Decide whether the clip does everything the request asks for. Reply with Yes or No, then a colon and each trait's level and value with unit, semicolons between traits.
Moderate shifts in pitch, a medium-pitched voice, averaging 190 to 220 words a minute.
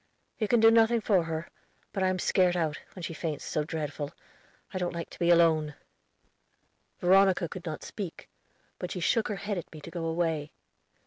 Yes: average, 3.1 semitones; medium, 175 Hz; average, 195 wpm